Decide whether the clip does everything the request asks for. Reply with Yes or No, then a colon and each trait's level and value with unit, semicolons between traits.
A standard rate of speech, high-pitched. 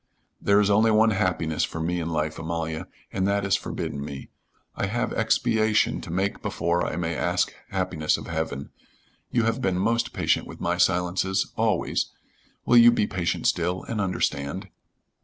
No: average, 170 wpm; very low, 90 Hz